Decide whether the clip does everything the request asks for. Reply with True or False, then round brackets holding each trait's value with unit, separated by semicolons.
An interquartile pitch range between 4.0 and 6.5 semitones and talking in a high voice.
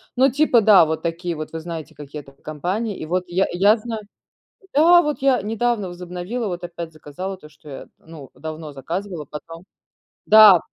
False (5.2 semitones; 175 Hz)